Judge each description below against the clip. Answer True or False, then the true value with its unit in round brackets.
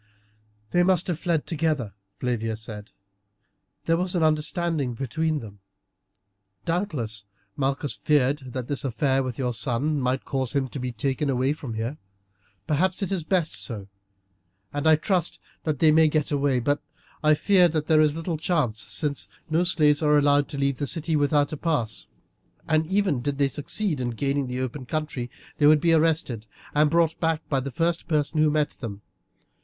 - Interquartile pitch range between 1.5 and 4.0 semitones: True (3.7 semitones)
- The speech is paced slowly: False (175 wpm)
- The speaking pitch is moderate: True (145 Hz)